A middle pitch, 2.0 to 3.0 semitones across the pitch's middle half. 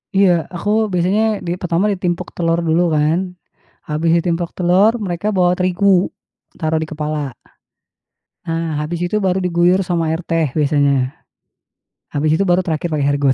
Yes: medium, 170 Hz; narrow, 2.6 semitones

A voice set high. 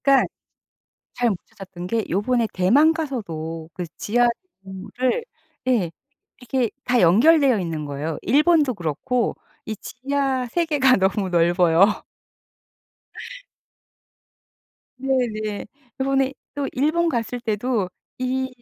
Yes: high, 240 Hz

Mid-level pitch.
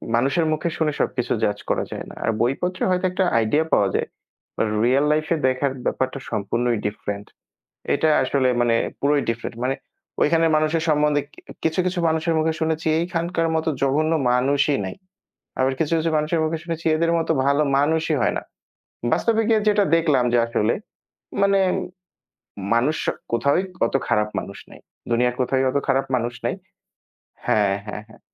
Yes: medium, 145 Hz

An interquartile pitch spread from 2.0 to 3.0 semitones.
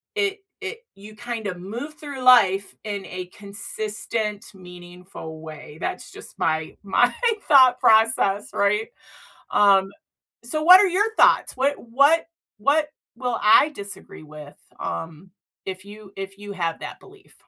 No: wide, 5.5 semitones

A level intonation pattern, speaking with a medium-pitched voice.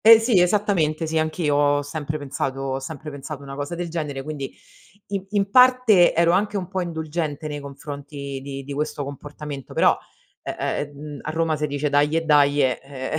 No: average, 3.1 semitones; medium, 150 Hz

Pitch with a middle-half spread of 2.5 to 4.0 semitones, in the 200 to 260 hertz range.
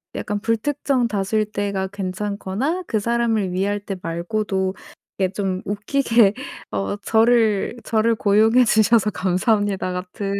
Yes: average, 2.8 semitones; high, 205 Hz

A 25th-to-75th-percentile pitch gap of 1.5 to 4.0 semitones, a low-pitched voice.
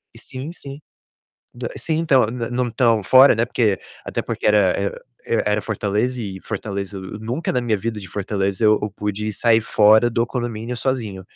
Yes: average, 2.9 semitones; low, 110 Hz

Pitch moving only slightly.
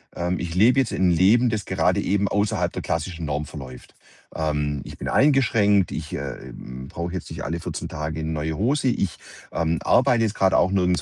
No: average, 4.7 semitones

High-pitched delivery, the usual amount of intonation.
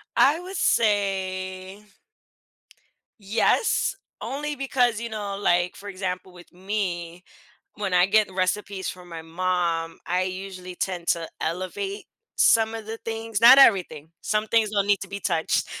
Yes: high, 195 Hz; average, 3.3 semitones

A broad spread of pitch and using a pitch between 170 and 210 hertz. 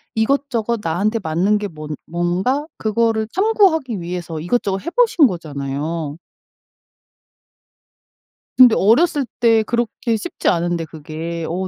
Yes: wide, 6.1 semitones; high, 205 Hz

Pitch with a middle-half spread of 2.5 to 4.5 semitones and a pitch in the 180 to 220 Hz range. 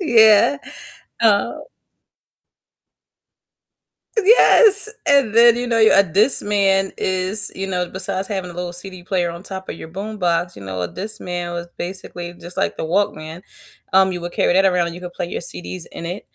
Yes: average, 2.9 semitones; high, 190 Hz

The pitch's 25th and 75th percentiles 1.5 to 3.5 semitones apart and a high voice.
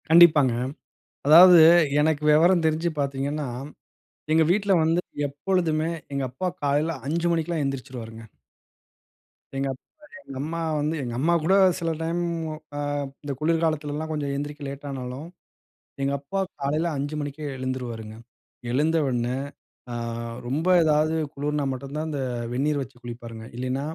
No: average, 2.9 semitones; medium, 145 Hz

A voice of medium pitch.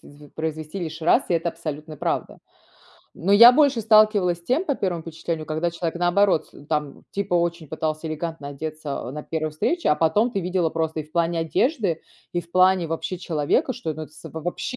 Yes: medium, 165 Hz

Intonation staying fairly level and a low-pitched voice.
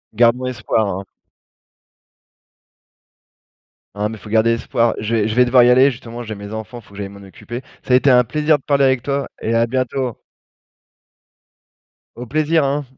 No: average, 3.1 semitones; low, 120 Hz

